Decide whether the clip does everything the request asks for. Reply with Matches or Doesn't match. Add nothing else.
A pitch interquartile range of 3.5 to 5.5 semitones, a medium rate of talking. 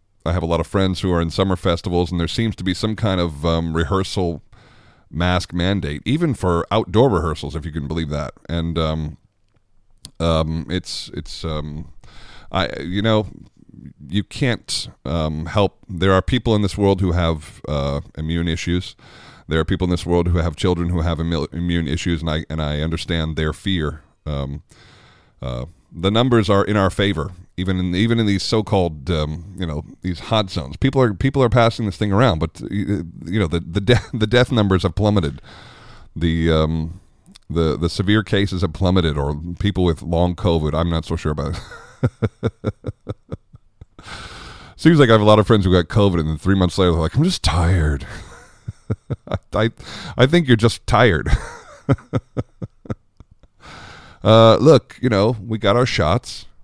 Matches